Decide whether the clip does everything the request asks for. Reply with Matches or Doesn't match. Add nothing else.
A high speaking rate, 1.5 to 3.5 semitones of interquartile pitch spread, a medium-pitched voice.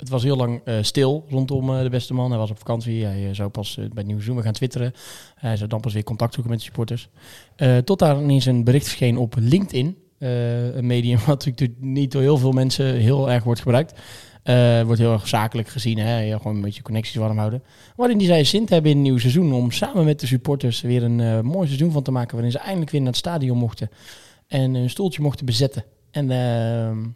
Doesn't match